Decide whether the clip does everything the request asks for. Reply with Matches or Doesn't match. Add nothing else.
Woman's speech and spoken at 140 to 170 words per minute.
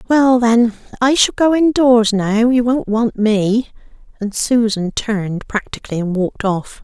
Matches